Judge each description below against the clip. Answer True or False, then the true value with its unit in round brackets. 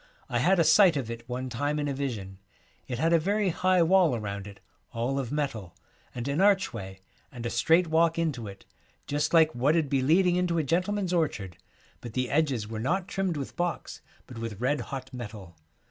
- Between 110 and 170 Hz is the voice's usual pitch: True (140 Hz)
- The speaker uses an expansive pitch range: True (6.2 semitones)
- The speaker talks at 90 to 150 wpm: False (205 wpm)